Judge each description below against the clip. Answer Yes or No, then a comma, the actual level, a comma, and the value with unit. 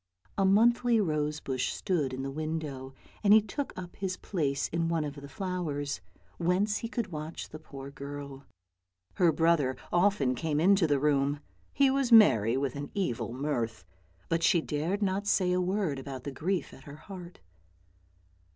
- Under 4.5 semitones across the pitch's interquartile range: No, average, 5.3 semitones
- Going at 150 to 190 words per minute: Yes, average, 170 wpm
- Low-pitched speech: No, medium, 160 Hz